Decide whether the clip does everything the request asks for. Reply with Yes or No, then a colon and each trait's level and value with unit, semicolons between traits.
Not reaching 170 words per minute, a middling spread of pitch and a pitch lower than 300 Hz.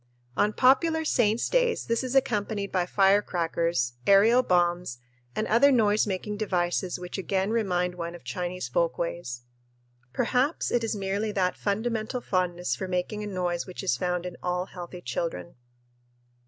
Yes: average, 150 wpm; average, 3.7 semitones; high, 190 Hz